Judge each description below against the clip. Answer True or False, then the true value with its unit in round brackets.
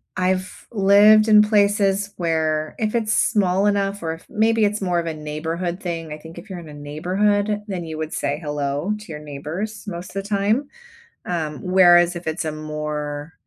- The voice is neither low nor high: True (180 Hz)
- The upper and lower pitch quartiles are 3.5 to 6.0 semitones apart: True (4.7 semitones)